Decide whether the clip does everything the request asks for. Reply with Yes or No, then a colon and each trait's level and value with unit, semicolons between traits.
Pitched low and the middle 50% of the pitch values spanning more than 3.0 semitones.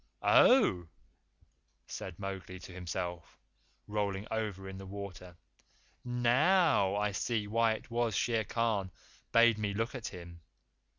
Yes: low, 105 Hz; average, 3.5 semitones